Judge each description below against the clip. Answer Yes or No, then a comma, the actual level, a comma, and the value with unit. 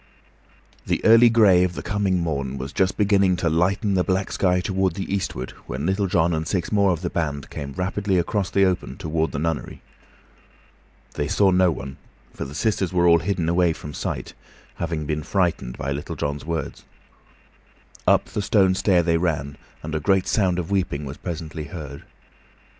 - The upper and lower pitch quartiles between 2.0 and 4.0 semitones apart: Yes, average, 3.7 semitones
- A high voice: No, very low, 90 Hz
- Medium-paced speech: Yes, average, 185 wpm